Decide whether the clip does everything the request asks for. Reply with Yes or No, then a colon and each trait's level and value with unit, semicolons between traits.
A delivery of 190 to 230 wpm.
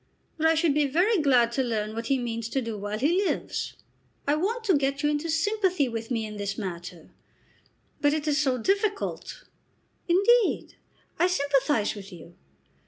No: average, 175 wpm